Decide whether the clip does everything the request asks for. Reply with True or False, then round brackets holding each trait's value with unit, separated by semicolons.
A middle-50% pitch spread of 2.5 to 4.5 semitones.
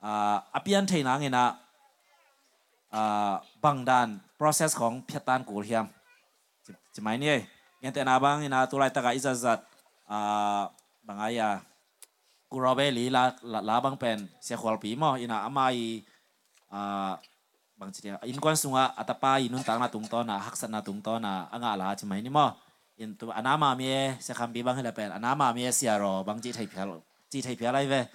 True (3.7 semitones)